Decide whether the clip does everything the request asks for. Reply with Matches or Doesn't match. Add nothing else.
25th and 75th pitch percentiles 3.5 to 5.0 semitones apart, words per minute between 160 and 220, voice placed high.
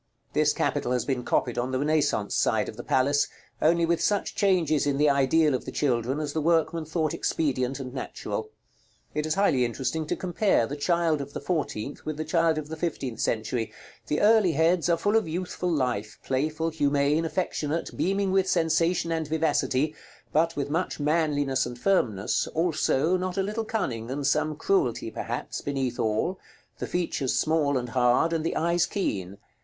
Doesn't match